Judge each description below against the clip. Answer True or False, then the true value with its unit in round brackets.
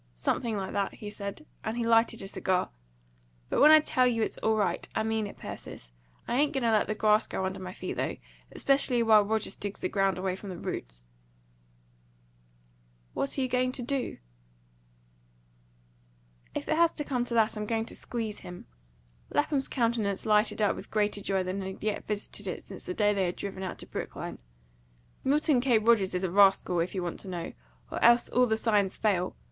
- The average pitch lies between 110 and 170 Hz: False (215 Hz)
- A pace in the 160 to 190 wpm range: False (205 wpm)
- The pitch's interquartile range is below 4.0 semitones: True (3.6 semitones)